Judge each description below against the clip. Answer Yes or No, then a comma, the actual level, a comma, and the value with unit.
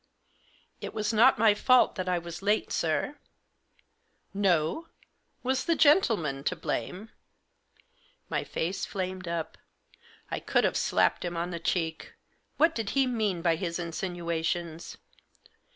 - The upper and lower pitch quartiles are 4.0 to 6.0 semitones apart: Yes, average, 4.7 semitones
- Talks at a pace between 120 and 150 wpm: Yes, average, 145 wpm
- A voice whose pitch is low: No, medium, 185 Hz